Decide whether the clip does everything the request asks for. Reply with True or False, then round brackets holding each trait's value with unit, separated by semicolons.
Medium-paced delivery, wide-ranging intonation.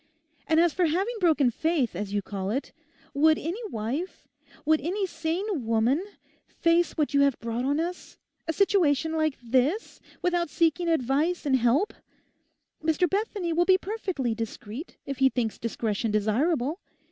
True (150 wpm; 6.0 semitones)